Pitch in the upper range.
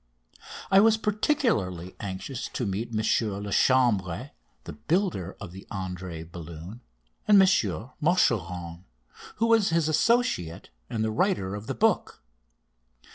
No: low, 110 Hz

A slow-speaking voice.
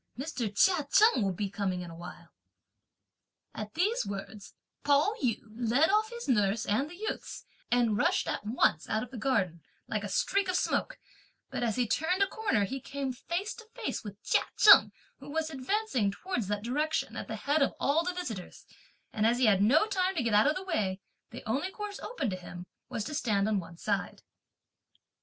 No: average, 200 wpm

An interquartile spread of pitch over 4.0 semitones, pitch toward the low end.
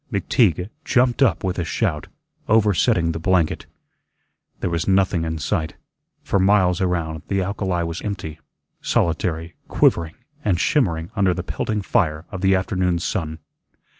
No: average, 3.2 semitones; very low, 90 Hz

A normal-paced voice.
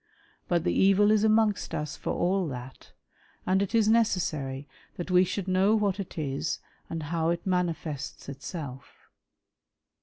Yes: average, 150 wpm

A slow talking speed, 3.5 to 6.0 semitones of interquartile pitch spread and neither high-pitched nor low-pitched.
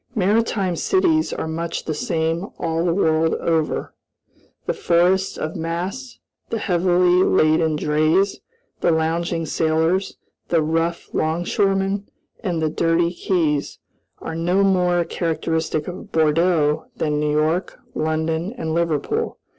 No: slow, 125 wpm; narrow, 2.5 semitones; medium, 170 Hz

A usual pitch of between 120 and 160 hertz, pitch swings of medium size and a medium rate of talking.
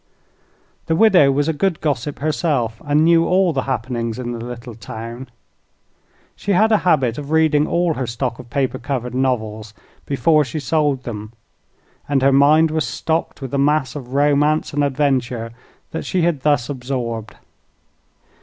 Yes: medium, 140 Hz; average, 4.1 semitones; average, 160 wpm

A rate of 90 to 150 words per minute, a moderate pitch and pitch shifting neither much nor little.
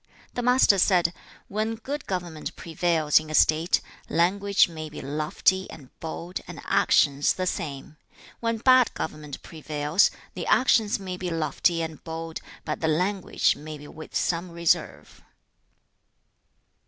Yes: average, 140 wpm; medium, 170 Hz; average, 3.6 semitones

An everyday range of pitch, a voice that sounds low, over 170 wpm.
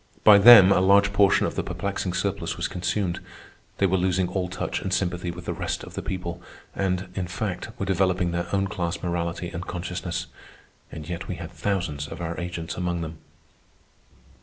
No: narrow, 1.9 semitones; very low, 90 Hz; average, 185 wpm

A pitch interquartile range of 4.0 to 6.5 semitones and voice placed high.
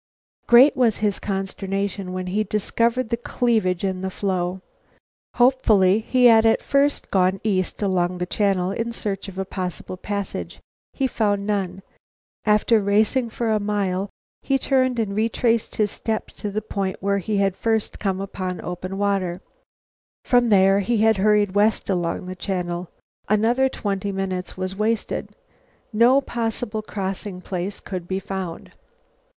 No: average, 2.9 semitones; high, 200 Hz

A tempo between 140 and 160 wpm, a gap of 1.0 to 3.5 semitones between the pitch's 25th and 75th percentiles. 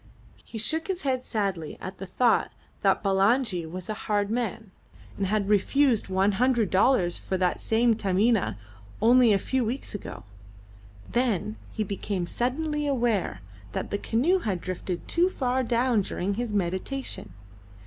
No: average, 150 wpm; average, 4.6 semitones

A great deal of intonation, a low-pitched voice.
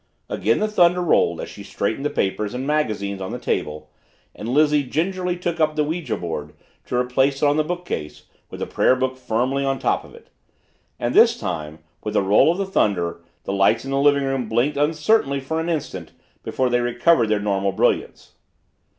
Yes: wide, 6.8 semitones; low, 130 Hz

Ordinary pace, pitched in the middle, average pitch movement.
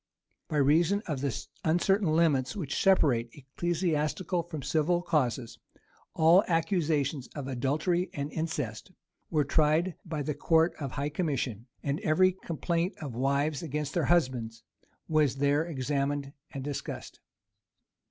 No: slow, 130 wpm; medium, 150 Hz; average, 3.5 semitones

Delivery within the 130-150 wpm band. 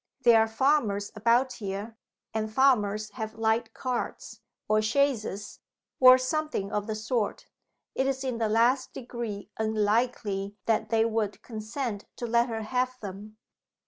Yes: average, 145 wpm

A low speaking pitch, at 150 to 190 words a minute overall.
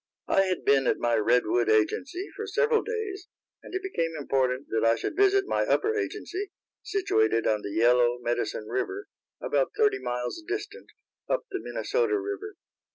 No: very high, 360 Hz; average, 160 wpm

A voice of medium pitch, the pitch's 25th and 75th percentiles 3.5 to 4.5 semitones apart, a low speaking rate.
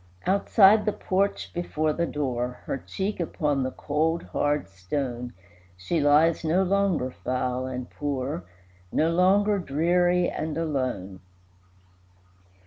No: medium, 155 Hz; wide, 5.6 semitones; slow, 120 wpm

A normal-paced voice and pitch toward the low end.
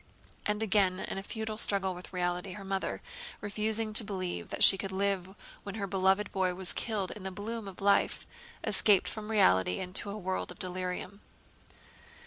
No: average, 175 wpm; high, 195 Hz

